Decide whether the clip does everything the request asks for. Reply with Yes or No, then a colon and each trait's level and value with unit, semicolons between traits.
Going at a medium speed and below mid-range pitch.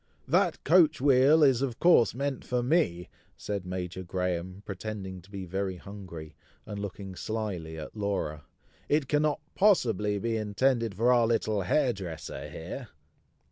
Yes: average, 145 wpm; low, 105 Hz